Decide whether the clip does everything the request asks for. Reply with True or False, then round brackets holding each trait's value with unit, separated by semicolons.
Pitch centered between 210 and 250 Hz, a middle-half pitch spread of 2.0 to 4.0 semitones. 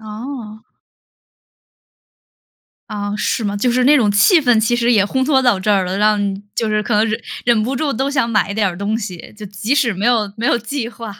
True (220 Hz; 3.0 semitones)